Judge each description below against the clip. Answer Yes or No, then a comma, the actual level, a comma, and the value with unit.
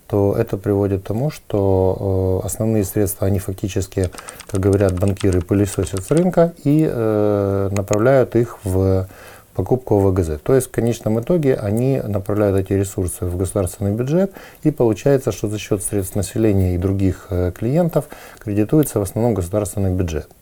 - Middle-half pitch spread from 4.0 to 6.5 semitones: No, average, 3.3 semitones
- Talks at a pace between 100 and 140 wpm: No, fast, 155 wpm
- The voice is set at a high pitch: No, low, 100 Hz